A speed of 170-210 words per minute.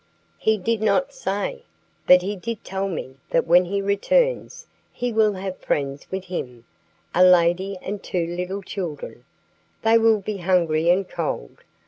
No: average, 155 wpm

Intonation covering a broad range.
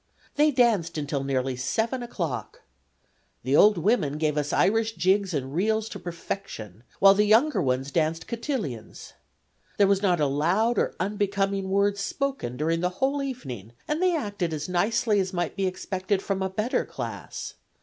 Yes: wide, 6.1 semitones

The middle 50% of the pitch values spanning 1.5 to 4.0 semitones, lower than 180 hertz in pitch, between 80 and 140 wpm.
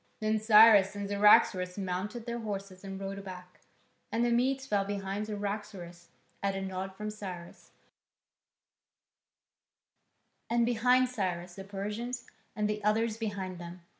No: narrow, 2.4 semitones; high, 205 Hz; slow, 135 wpm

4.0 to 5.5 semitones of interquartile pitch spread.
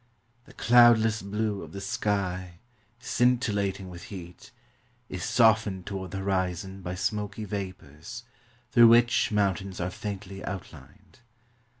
No: average, 2.9 semitones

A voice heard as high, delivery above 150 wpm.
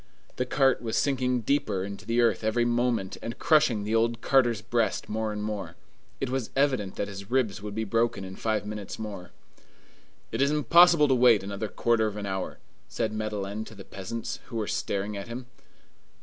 No: low, 110 Hz; average, 190 wpm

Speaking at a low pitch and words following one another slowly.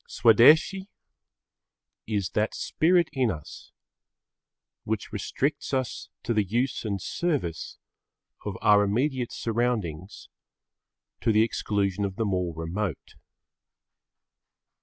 Yes: low, 110 Hz; slow, 100 wpm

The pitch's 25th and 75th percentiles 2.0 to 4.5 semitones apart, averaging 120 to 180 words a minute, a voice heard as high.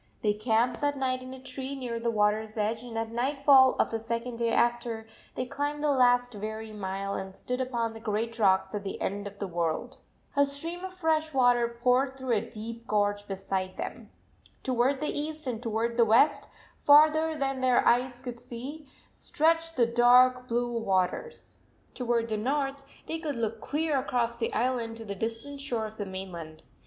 No: average, 3.5 semitones; average, 190 wpm; high, 240 Hz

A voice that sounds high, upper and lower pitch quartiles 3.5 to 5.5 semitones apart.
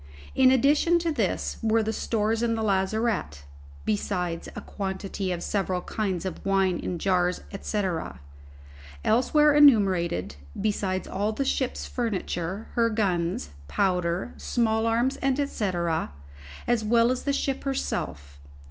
Yes: high, 210 Hz; average, 4.5 semitones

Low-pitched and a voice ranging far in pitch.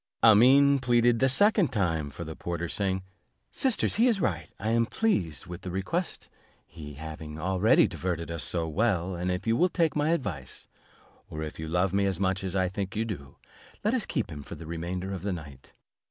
Yes: very low, 95 Hz; wide, 6.1 semitones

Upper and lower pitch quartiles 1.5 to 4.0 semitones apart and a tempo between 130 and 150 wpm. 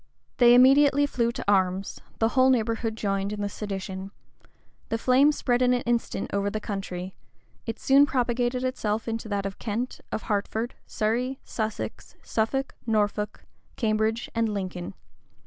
Yes: average, 3.4 semitones; average, 145 wpm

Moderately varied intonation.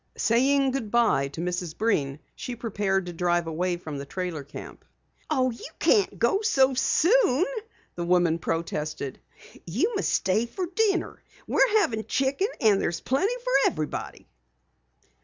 No: wide, 8.0 semitones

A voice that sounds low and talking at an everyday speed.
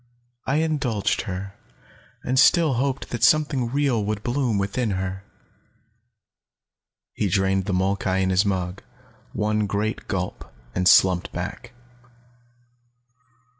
No: low, 105 Hz; slow, 115 wpm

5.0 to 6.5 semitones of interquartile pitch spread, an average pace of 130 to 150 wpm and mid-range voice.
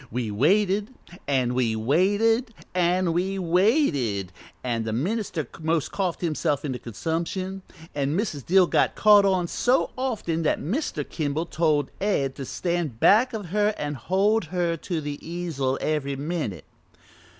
Yes: wide, 5.6 semitones; average, 145 wpm; medium, 170 Hz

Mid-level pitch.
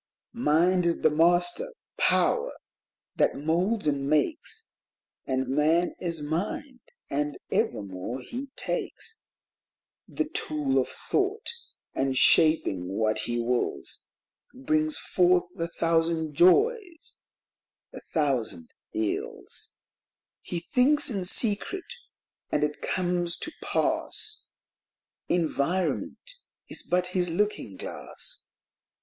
Yes: medium, 175 Hz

